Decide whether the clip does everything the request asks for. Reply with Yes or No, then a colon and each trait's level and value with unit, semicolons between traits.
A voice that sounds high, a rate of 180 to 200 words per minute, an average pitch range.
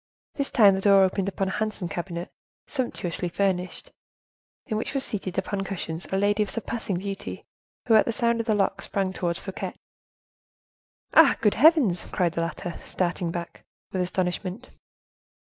No: high, 195 Hz; average, 165 wpm; average, 3.2 semitones